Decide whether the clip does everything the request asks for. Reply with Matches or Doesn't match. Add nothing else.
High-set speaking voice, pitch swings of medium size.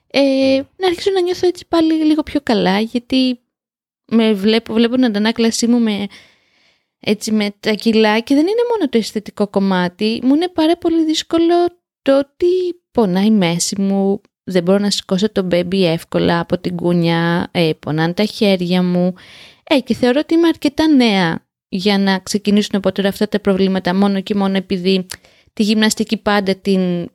Doesn't match